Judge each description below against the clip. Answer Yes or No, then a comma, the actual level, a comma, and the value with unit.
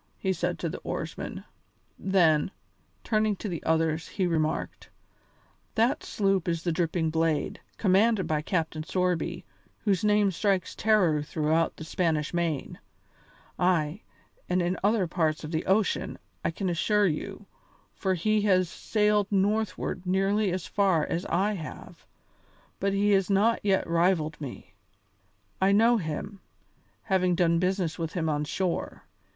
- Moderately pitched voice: Yes, medium, 180 Hz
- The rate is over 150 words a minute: No, average, 145 wpm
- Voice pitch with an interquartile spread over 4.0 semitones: No, average, 3.5 semitones